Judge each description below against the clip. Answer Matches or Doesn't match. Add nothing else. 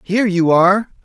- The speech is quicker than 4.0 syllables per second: Matches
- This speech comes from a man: Matches